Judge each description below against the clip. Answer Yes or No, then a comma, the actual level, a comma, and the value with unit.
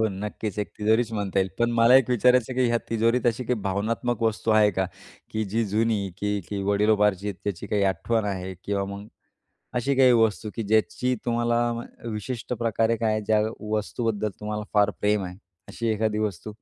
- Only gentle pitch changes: Yes, narrow, 2.2 semitones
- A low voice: Yes, low, 110 Hz